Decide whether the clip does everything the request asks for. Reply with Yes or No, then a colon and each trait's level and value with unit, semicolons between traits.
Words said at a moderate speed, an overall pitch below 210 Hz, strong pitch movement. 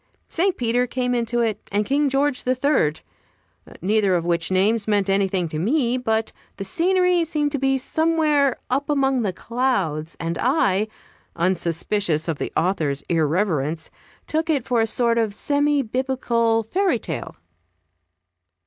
No: average, 150 wpm; high, 230 Hz; wide, 6.5 semitones